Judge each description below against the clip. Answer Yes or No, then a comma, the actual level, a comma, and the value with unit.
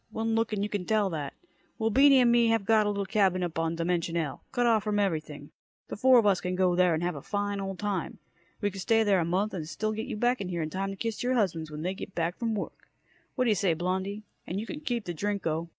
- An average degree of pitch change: Yes, average, 4.0 semitones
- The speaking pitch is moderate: No, high, 195 Hz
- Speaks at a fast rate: Yes, fast, 265 wpm